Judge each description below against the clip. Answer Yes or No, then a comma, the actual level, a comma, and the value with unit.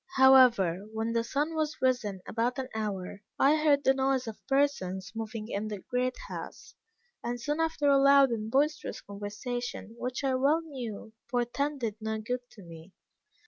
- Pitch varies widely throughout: No, average, 4.2 semitones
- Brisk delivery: No, average, 165 wpm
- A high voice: Yes, high, 245 Hz